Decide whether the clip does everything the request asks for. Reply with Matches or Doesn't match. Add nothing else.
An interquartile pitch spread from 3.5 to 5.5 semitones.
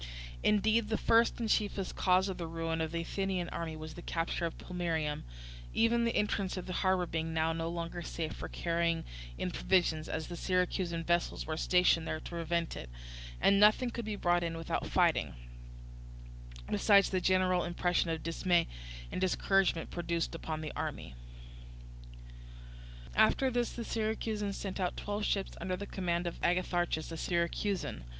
Doesn't match